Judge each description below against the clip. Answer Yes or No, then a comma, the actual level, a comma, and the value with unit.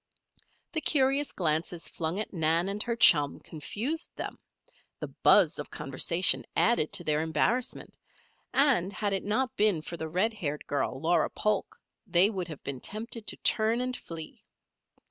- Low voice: No, high, 190 Hz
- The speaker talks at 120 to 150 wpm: No, average, 160 wpm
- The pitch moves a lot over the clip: Yes, wide, 6.3 semitones